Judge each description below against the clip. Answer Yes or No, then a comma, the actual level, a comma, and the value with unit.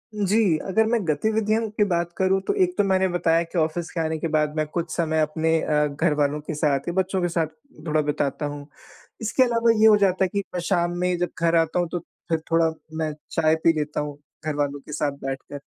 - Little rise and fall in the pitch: No, average, 3.8 semitones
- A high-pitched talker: No, medium, 165 Hz